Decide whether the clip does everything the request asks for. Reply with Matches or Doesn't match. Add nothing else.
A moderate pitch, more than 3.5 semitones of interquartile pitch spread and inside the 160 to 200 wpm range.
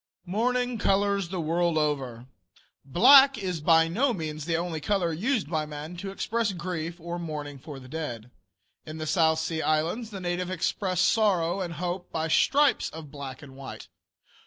Matches